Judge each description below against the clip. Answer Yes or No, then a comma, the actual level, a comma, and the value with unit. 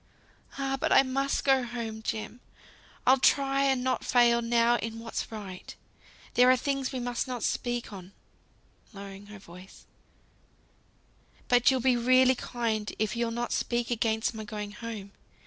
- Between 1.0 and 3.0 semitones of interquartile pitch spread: Yes, average, 2.7 semitones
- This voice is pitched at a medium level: No, high, 235 Hz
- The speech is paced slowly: No, average, 155 wpm